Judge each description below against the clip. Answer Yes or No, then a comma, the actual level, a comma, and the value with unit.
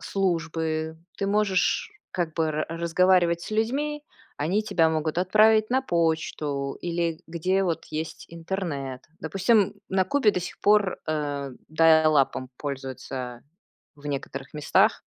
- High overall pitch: No, medium, 165 Hz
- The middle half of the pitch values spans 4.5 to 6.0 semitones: No, average, 4.0 semitones